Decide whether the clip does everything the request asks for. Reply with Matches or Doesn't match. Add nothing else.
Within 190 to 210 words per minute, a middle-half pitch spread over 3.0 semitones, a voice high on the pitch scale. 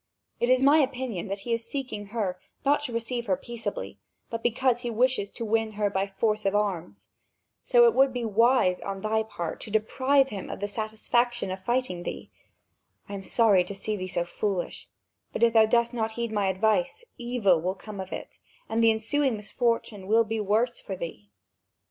Matches